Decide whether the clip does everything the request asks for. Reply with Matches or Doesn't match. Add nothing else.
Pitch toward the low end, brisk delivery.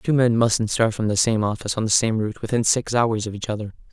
Matches